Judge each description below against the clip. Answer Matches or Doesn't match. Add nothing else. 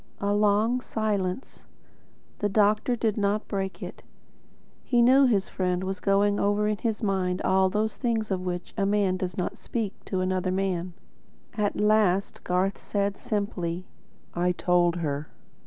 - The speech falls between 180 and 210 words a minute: Doesn't match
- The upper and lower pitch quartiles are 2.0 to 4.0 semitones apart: Matches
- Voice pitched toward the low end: Doesn't match